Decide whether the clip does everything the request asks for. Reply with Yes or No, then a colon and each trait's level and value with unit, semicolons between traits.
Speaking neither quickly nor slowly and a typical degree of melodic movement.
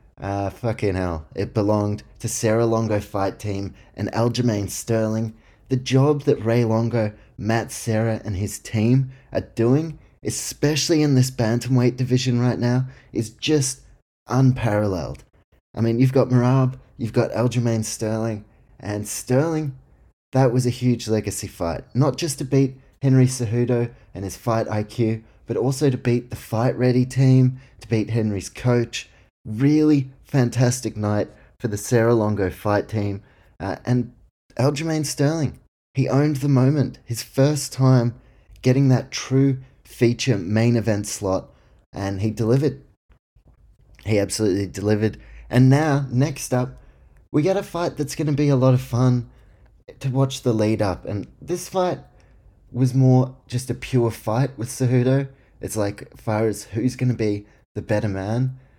Yes: average, 155 wpm; average, 3.5 semitones